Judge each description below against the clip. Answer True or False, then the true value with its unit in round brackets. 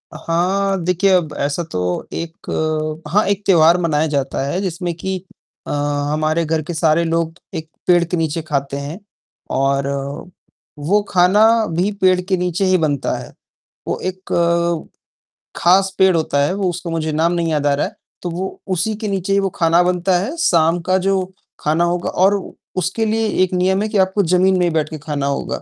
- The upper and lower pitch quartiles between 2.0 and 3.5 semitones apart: True (3.1 semitones)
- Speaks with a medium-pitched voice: True (170 Hz)